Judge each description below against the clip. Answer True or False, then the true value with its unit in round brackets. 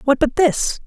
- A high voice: True (280 Hz)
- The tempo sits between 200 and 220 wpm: True (210 wpm)